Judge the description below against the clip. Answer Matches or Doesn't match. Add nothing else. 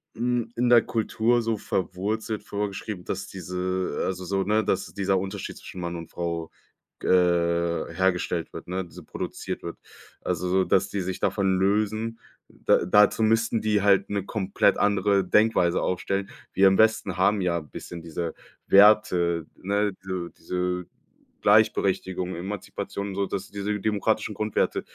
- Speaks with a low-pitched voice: Matches